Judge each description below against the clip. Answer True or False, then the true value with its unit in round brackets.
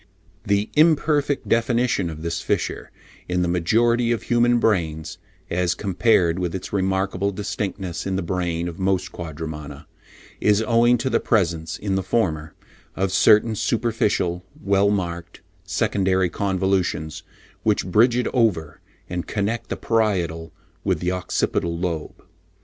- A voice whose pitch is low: True (95 Hz)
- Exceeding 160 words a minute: False (135 wpm)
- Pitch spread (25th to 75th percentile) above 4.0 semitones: True (4.5 semitones)